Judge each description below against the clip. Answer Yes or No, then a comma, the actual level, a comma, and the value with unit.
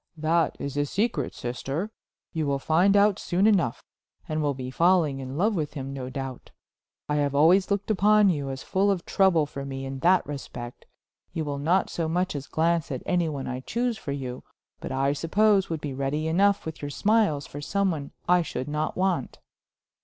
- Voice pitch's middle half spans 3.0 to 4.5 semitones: No, average, 5.2 semitones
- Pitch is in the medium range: Yes, medium, 155 Hz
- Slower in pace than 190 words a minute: No, average, 200 wpm